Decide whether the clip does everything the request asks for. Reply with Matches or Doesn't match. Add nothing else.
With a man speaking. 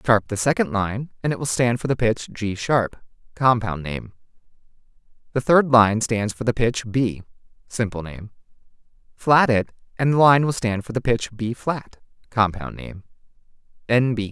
Matches